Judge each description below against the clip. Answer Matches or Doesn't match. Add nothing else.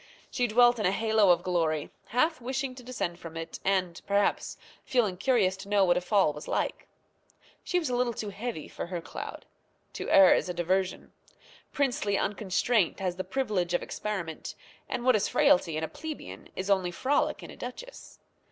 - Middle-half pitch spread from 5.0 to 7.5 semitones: Matches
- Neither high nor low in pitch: Doesn't match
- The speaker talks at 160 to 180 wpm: Doesn't match